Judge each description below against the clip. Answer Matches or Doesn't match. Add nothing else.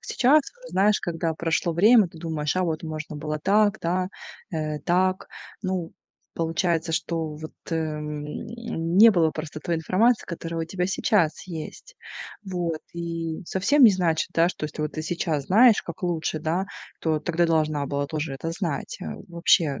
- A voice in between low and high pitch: Matches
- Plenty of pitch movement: Doesn't match